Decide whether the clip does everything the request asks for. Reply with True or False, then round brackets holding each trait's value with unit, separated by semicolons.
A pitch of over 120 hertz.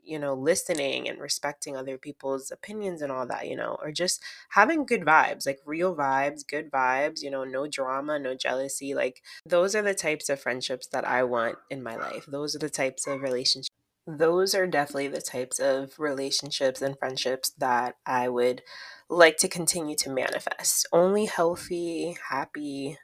True (140 Hz)